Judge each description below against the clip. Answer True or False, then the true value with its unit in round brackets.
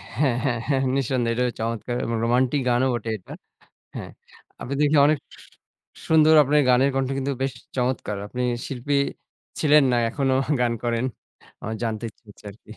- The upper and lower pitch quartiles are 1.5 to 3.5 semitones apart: True (2.8 semitones)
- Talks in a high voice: False (125 Hz)